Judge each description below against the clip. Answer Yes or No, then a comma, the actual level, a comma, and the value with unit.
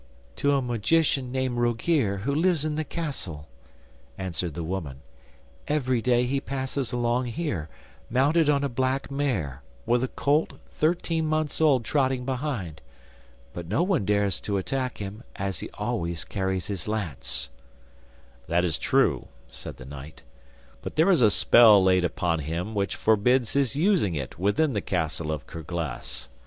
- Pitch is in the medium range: No, low, 120 Hz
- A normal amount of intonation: No, wide, 7.3 semitones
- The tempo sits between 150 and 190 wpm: Yes, average, 155 wpm